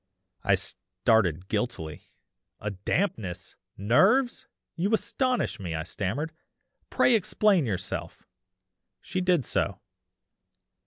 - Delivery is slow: Yes, slow, 95 wpm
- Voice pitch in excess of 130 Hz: No, low, 115 Hz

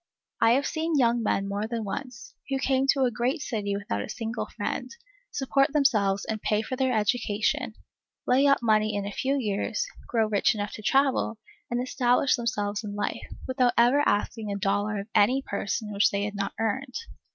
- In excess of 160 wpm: Yes, average, 190 wpm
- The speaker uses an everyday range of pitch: Yes, average, 4.1 semitones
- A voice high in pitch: Yes, high, 225 Hz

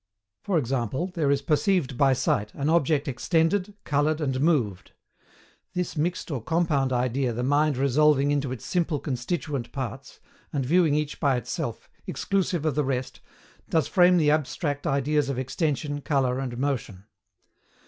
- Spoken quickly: No, average, 150 wpm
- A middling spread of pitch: Yes, average, 3.3 semitones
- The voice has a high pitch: No, medium, 145 Hz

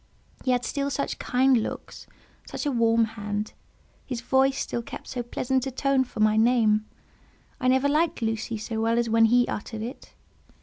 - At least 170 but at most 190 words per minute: Yes, average, 180 wpm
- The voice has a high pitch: Yes, high, 240 Hz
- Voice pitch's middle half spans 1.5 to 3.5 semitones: Yes, average, 2.8 semitones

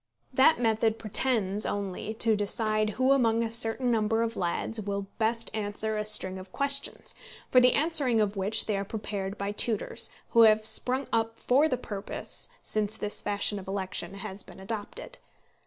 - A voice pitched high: Yes, high, 215 Hz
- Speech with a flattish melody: Yes, narrow, 2.2 semitones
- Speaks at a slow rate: No, average, 170 wpm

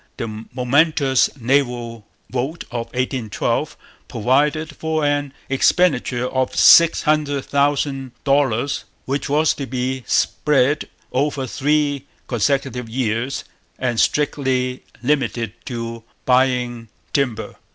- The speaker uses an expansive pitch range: No, average, 2.8 semitones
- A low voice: Yes, low, 130 Hz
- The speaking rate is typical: No, slow, 100 wpm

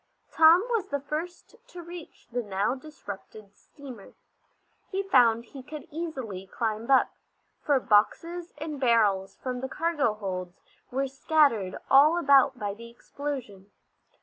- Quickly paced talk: No, slow, 135 wpm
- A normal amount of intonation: No, wide, 6.3 semitones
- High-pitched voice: Yes, very high, 265 Hz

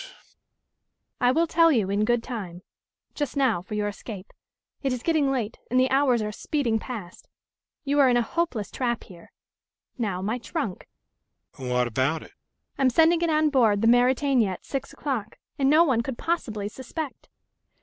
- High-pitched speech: Yes, high, 245 Hz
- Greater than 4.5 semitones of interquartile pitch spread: Yes, average, 4.9 semitones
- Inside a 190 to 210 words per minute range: No, average, 175 wpm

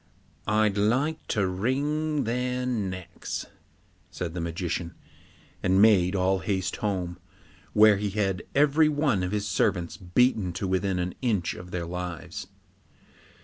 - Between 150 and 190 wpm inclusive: No, slow, 135 wpm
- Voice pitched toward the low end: Yes, low, 100 Hz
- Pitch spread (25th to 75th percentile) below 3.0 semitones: No, average, 5.0 semitones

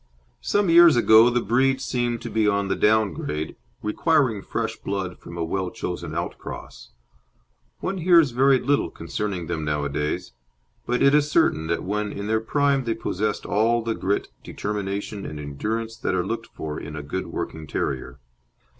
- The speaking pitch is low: Yes, low, 105 Hz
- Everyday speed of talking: Yes, average, 170 wpm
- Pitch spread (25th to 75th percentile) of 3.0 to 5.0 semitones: No, wide, 5.4 semitones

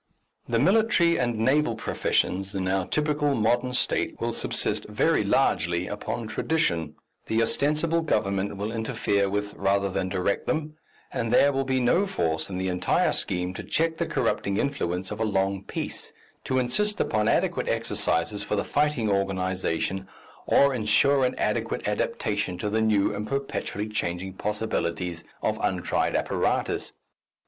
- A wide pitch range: Yes, wide, 6.0 semitones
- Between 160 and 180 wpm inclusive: No, average, 150 wpm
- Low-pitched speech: Yes, low, 105 Hz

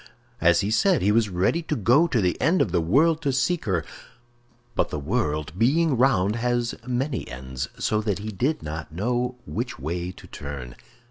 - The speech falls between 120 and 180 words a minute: No, average, 190 wpm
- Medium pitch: No, low, 110 Hz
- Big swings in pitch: Yes, wide, 7.7 semitones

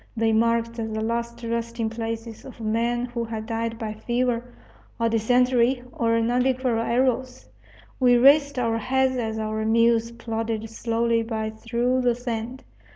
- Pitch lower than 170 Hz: No, high, 230 Hz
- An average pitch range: No, narrow, 1.4 semitones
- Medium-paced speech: Yes, average, 145 wpm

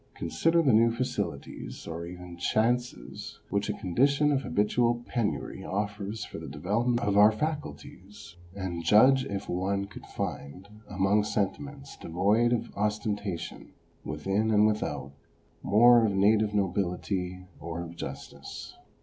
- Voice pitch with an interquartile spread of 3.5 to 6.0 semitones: Yes, average, 4.1 semitones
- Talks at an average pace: No, slow, 130 wpm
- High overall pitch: No, low, 105 Hz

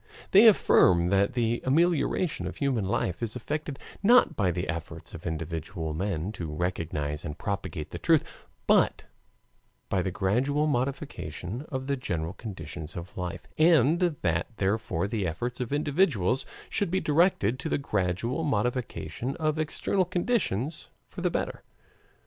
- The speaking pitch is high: No, low, 115 Hz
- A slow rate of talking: No, average, 145 wpm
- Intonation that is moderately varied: No, wide, 8.9 semitones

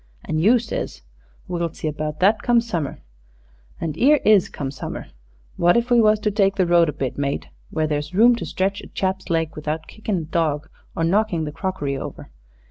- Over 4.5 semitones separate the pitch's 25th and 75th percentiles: Yes, wide, 5.6 semitones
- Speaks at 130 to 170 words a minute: No, average, 200 wpm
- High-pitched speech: No, medium, 170 Hz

